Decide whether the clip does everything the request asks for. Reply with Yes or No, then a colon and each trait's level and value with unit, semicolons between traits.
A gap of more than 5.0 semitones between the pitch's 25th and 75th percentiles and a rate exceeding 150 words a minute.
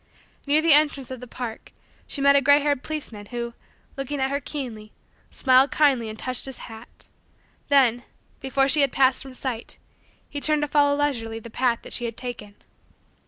No: average, 3.2 semitones; average, 185 wpm